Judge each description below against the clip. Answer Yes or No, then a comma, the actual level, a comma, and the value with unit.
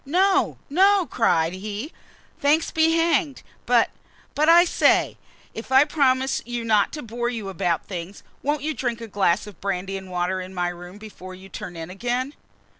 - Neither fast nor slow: Yes, average, 180 wpm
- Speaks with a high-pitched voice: Yes, high, 230 Hz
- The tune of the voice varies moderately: No, wide, 7.7 semitones